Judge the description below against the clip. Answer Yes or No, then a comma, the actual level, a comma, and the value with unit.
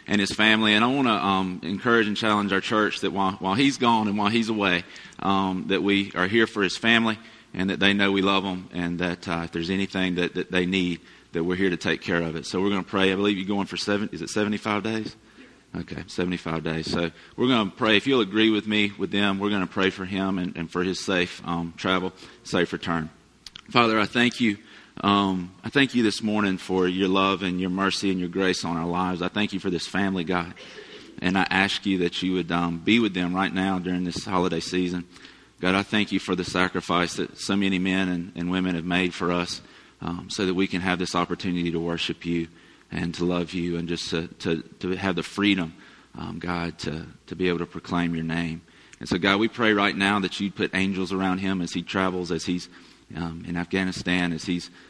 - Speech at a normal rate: No, fast, 240 wpm